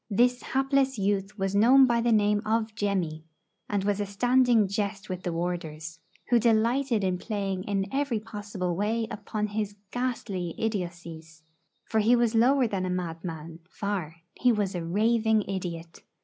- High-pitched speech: Yes, high, 205 Hz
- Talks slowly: No, average, 160 wpm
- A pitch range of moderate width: Yes, average, 3.9 semitones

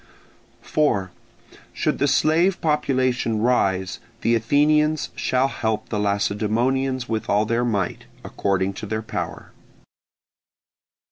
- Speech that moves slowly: Yes, slow, 110 wpm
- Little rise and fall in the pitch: No, average, 4.7 semitones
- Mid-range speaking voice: No, low, 115 Hz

